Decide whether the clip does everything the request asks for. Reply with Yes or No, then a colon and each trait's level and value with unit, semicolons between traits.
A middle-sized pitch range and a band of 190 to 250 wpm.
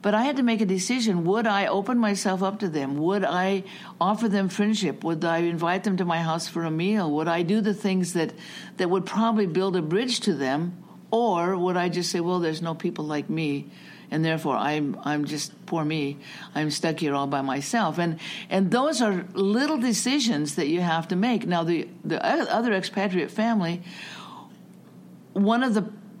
Yes: average, 4.1 semitones; average, 200 wpm